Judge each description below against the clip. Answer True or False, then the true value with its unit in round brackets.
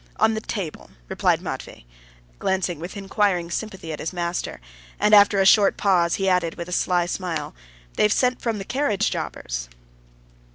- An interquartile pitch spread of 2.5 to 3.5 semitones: True (3.2 semitones)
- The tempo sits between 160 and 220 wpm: True (165 wpm)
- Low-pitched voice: False (190 Hz)